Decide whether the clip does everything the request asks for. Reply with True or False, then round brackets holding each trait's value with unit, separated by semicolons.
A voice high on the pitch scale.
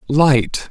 False (140 Hz)